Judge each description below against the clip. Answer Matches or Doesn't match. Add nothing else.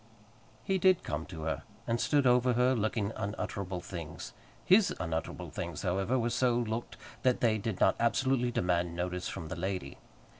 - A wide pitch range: Matches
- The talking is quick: Doesn't match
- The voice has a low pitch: Matches